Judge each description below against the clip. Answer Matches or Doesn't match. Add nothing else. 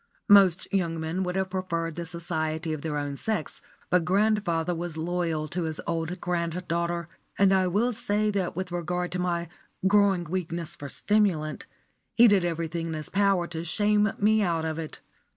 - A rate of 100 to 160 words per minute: Doesn't match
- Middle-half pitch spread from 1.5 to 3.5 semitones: Matches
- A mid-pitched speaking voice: Matches